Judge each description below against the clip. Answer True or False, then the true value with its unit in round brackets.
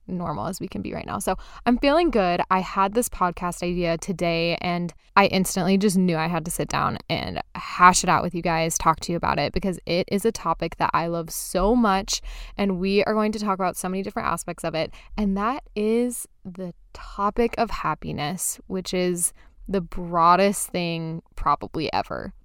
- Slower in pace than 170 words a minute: False (205 wpm)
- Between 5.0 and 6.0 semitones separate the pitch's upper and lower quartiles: False (2.9 semitones)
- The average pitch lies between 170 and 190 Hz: True (185 Hz)